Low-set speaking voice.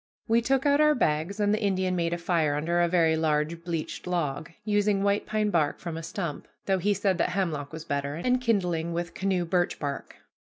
No: medium, 175 Hz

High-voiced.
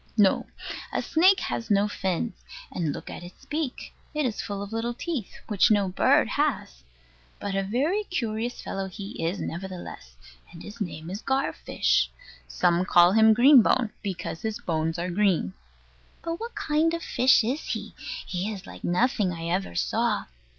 Yes: high, 205 Hz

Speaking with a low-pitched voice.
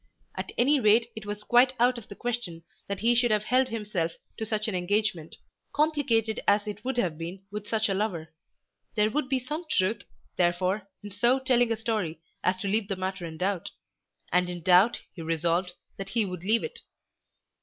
No: high, 210 Hz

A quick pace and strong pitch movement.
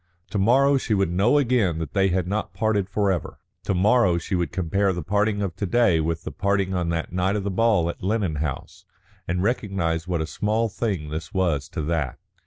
No: fast, 210 wpm; average, 3.7 semitones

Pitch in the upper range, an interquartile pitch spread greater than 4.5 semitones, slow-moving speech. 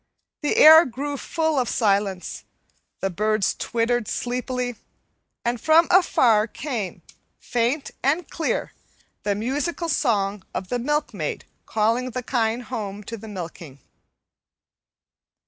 Yes: high, 240 Hz; average, 4.9 semitones; slow, 115 wpm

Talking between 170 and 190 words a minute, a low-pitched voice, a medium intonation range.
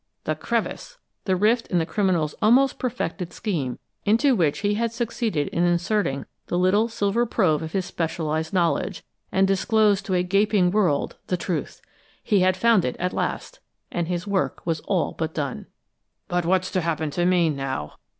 No: average, 175 wpm; medium, 185 Hz; average, 4.1 semitones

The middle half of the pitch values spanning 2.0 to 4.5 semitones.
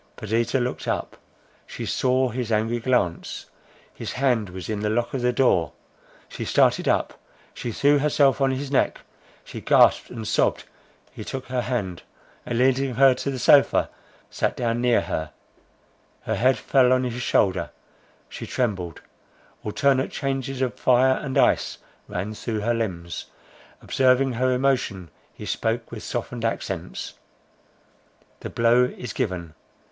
Yes: average, 3.4 semitones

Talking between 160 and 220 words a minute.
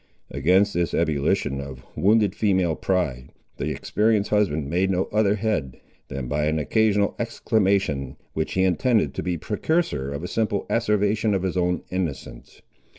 No: average, 150 wpm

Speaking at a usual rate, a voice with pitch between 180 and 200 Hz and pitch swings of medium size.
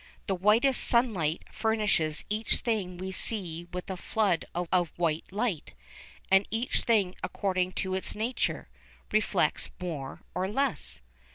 No: slow, 130 wpm; high, 190 Hz; average, 3.6 semitones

